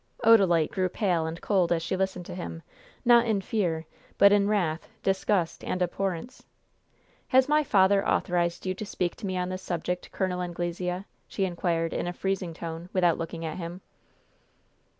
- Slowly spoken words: No, average, 170 wpm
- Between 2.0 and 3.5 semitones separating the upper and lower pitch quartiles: Yes, narrow, 2.4 semitones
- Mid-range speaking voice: Yes, medium, 180 Hz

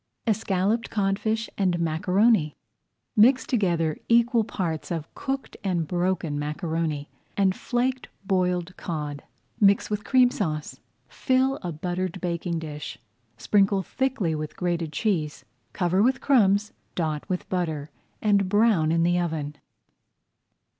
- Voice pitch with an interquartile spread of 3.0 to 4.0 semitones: No, average, 4.8 semitones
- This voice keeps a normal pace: No, slow, 125 wpm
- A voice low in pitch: No, medium, 185 Hz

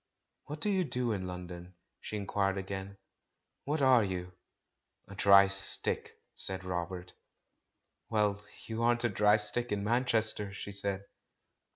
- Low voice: Yes, low, 100 Hz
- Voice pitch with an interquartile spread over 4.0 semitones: No, average, 3.3 semitones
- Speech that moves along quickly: No, average, 140 wpm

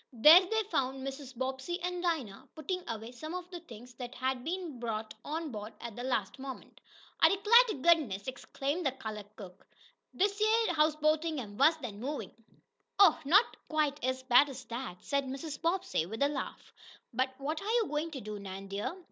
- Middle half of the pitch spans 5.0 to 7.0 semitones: Yes, wide, 5.5 semitones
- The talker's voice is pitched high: Yes, very high, 275 Hz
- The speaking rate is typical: Yes, average, 190 wpm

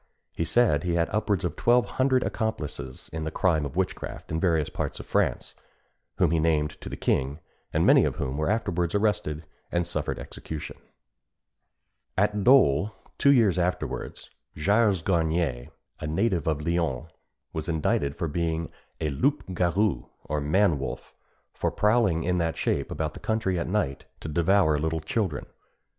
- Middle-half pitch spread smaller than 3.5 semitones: No, average, 4.8 semitones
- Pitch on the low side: Yes, very low, 85 Hz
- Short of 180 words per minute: Yes, average, 165 wpm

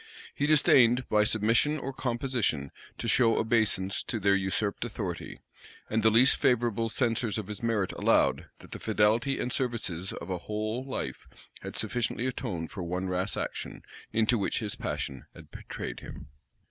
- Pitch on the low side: Yes, low, 110 Hz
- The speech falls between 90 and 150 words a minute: No, average, 160 wpm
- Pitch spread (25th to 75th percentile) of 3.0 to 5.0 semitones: Yes, average, 3.5 semitones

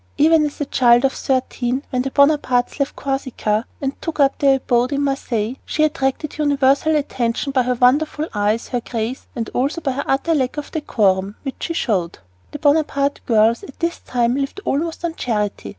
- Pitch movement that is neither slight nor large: Yes, average, 3.4 semitones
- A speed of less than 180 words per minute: No, average, 185 wpm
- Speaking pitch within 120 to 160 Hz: No, very high, 270 Hz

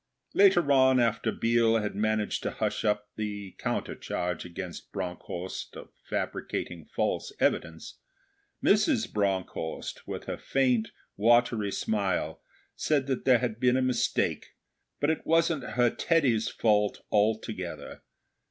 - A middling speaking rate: No, slow, 125 wpm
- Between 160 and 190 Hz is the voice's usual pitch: No, low, 110 Hz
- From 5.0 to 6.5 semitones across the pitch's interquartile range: No, average, 4.2 semitones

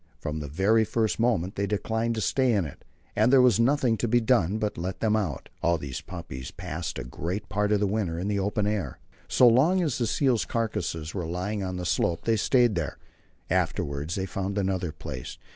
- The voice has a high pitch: No, low, 100 Hz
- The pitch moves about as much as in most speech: Yes, average, 4.8 semitones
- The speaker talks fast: Yes, fast, 215 wpm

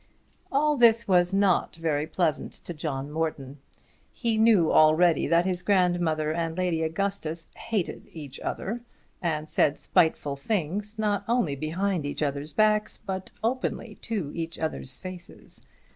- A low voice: No, medium, 175 Hz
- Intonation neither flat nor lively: Yes, average, 4.6 semitones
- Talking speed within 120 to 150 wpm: Yes, average, 140 wpm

